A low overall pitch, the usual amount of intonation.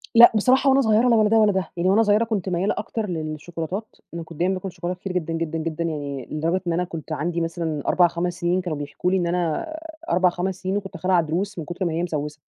No: medium, 175 Hz; average, 3.1 semitones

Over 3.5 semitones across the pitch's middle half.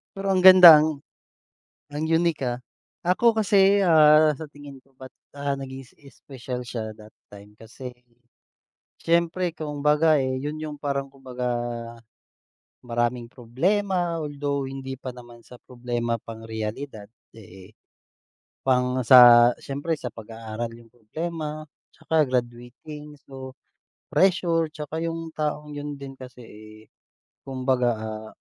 Yes: average, 4.4 semitones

